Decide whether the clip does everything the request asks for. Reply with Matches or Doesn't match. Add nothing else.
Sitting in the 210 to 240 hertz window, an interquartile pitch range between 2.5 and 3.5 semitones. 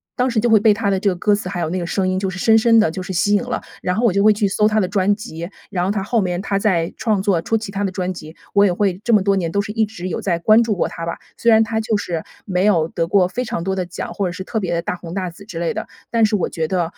Doesn't match